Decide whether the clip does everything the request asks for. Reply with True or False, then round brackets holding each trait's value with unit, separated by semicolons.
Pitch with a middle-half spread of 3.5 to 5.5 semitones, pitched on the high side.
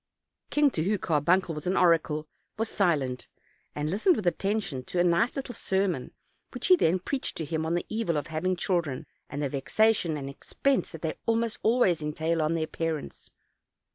False (5.0 semitones; 170 Hz)